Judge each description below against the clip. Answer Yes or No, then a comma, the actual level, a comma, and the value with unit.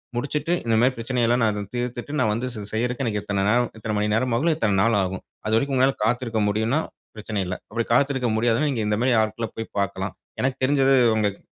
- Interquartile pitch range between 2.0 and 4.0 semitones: Yes, average, 3.1 semitones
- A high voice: No, low, 115 Hz